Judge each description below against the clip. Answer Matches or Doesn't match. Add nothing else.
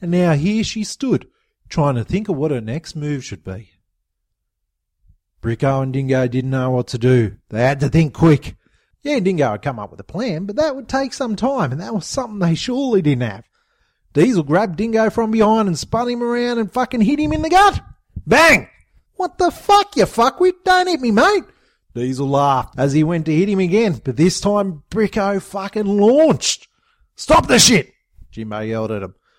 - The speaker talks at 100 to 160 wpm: Doesn't match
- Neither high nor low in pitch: Matches